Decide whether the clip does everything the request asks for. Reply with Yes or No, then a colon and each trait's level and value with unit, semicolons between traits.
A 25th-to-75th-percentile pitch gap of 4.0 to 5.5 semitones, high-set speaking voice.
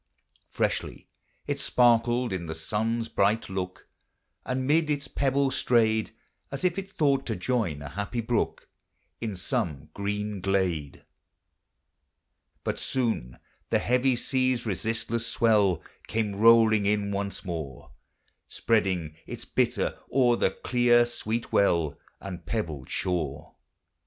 No: average, 4.6 semitones; low, 110 Hz